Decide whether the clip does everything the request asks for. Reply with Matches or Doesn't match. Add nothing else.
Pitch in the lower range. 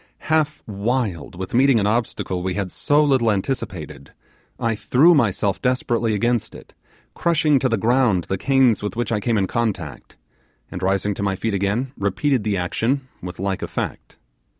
Matches